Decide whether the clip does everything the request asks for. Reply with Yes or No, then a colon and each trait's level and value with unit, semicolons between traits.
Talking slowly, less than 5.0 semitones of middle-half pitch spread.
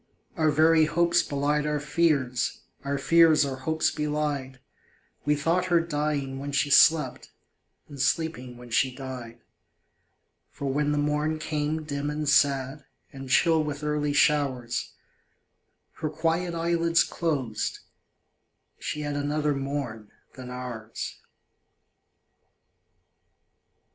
Yes: slow, 115 wpm; narrow, 2.5 semitones